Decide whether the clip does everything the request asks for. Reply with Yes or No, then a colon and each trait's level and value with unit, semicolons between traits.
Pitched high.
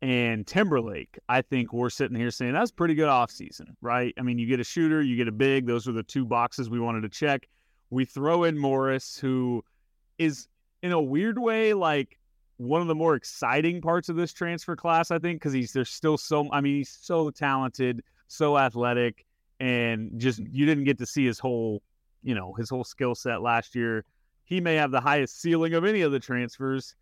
No: low, 130 Hz